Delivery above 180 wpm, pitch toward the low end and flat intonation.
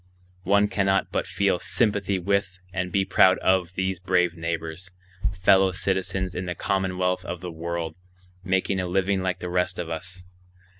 No: average, 160 wpm; very low, 90 Hz; narrow, 1.3 semitones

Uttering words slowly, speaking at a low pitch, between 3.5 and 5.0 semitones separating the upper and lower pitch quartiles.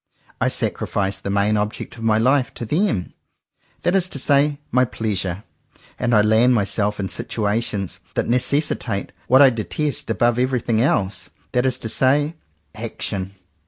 No: average, 160 wpm; low, 115 Hz; average, 4.1 semitones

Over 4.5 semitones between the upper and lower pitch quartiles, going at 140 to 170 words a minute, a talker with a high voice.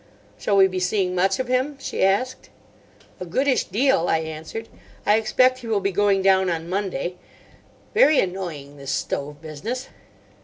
Yes: average, 4.9 semitones; average, 160 wpm; high, 195 Hz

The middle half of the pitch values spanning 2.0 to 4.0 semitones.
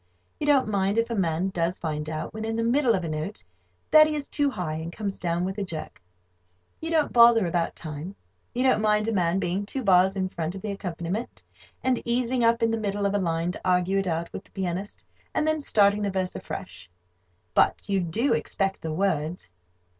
No: average, 4.8 semitones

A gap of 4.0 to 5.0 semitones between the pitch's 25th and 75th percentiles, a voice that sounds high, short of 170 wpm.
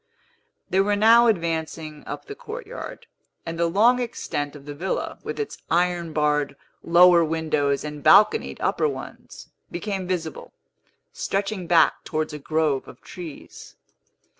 No: average, 4.6 semitones; medium, 170 Hz; average, 140 wpm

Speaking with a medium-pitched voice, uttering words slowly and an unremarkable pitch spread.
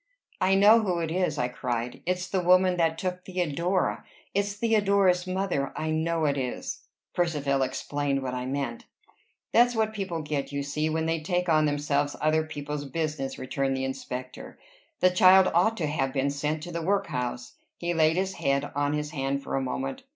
No: medium, 155 Hz; average, 185 wpm; average, 4.7 semitones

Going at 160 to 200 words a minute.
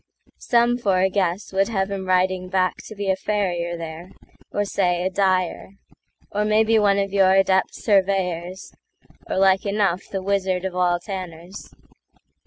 No: average, 145 wpm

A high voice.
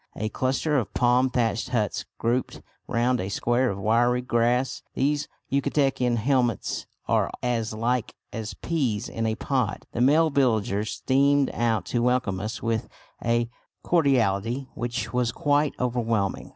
No: low, 120 Hz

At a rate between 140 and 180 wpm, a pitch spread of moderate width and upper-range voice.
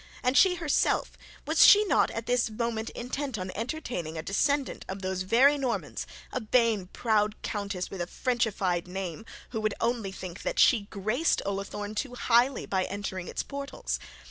Yes: average, 170 wpm; average, 4.6 semitones; high, 215 Hz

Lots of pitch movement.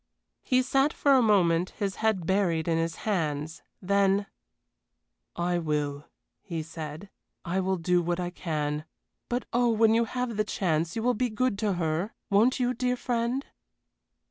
Yes: wide, 5.7 semitones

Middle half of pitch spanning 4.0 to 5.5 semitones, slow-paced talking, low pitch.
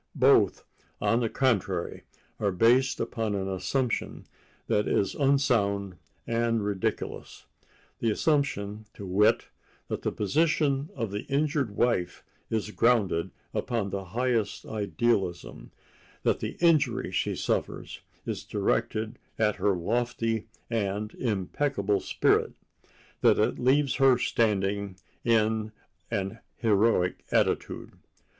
No: average, 3.6 semitones; slow, 105 wpm; low, 110 Hz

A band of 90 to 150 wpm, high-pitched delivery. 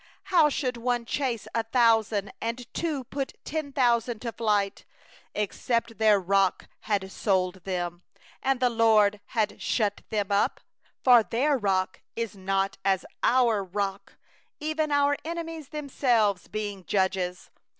Yes: average, 140 wpm; high, 225 Hz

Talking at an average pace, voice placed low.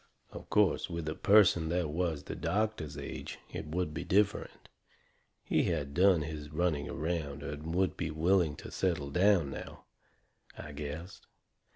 Yes: average, 155 wpm; very low, 80 Hz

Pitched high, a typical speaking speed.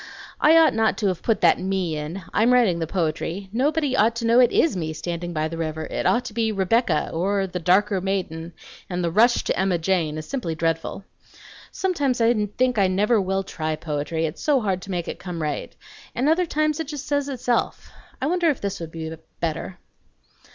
No: high, 195 Hz; fast, 210 wpm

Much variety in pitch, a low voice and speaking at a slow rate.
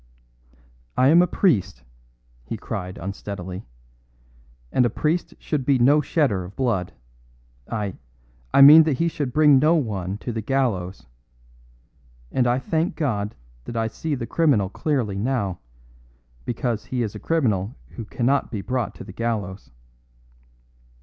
No: wide, 6.0 semitones; low, 120 Hz; average, 145 wpm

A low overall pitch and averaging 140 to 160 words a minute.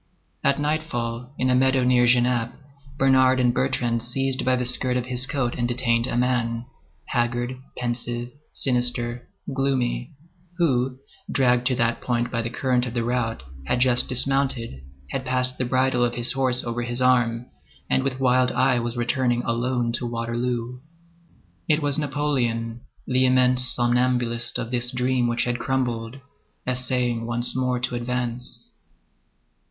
Yes: low, 125 Hz; average, 150 wpm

